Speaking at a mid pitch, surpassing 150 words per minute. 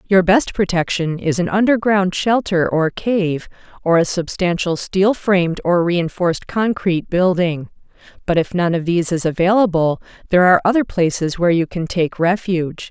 Yes: medium, 180 Hz; average, 160 wpm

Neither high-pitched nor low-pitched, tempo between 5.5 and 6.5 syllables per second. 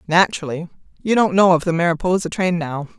Yes: medium, 175 Hz; 6.2 syllables/s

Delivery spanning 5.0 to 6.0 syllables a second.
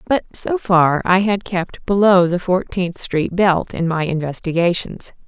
No: 4.1 syllables/s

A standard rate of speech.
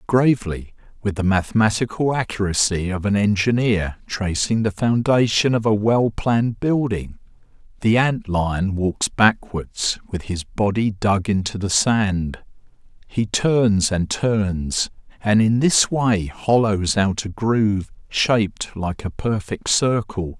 No: slow, 130 wpm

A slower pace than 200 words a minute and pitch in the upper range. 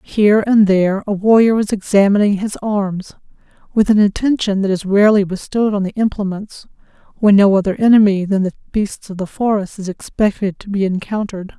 Yes: average, 175 wpm; high, 200 Hz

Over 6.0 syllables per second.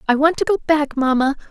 Yes: 6.3 syllables/s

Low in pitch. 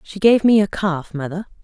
No: high, 190 Hz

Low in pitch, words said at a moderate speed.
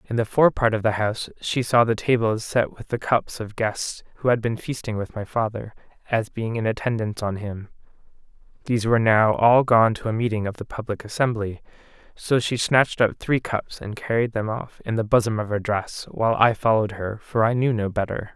No: low, 110 Hz; fast, 220 wpm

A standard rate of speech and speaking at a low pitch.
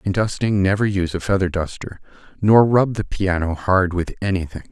Yes: average, 180 wpm; very low, 95 Hz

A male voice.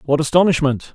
Yes: male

